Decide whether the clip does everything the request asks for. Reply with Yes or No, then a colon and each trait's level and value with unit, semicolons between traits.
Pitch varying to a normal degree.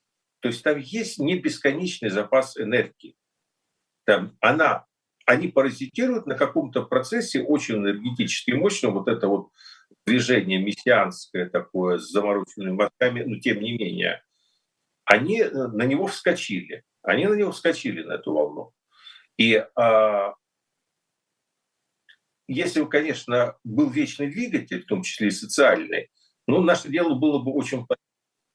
No: wide, 8.6 semitones